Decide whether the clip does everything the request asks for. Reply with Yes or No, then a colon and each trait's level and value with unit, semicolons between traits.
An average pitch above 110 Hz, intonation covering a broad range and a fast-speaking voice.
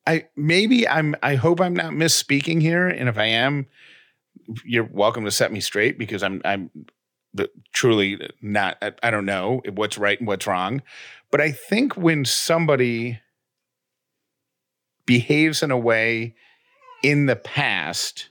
No: low, 135 Hz; wide, 5.7 semitones; average, 150 wpm